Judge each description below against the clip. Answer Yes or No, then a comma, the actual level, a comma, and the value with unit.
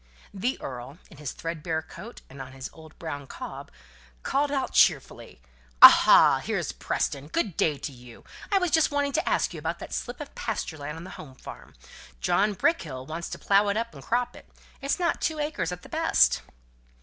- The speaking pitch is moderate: Yes, medium, 180 Hz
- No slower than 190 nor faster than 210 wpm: Yes, average, 200 wpm